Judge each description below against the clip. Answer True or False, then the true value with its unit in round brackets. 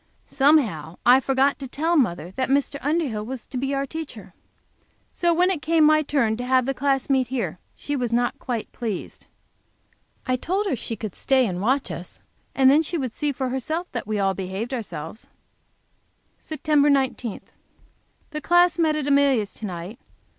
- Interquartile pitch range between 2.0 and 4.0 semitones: False (4.5 semitones)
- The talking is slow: False (180 wpm)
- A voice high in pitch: True (265 Hz)